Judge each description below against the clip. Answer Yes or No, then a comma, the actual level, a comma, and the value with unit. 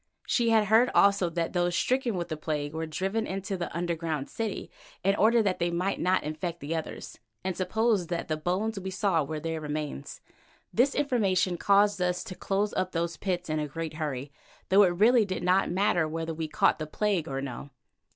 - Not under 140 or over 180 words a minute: No, fast, 205 wpm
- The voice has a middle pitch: Yes, medium, 180 Hz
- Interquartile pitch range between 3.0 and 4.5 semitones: Yes, average, 3.9 semitones